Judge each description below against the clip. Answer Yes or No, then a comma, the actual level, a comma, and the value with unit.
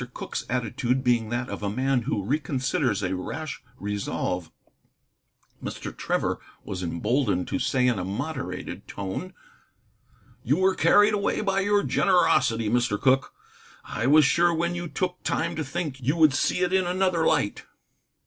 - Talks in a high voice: No, low, 135 Hz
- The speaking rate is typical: Yes, average, 155 wpm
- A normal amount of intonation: No, wide, 7.5 semitones